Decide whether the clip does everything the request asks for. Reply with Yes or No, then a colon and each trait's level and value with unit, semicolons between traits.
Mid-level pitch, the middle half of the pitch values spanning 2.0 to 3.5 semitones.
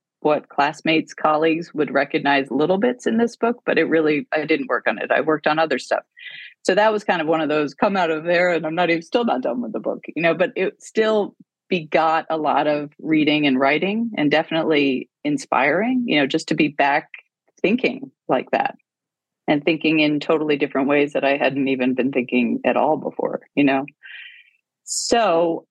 No: medium, 160 Hz; average, 3.9 semitones